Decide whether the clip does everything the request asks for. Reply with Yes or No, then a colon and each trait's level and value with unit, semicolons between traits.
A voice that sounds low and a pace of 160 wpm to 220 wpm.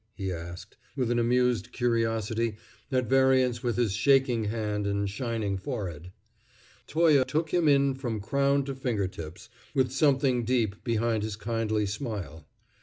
No: low, 115 Hz; average, 140 wpm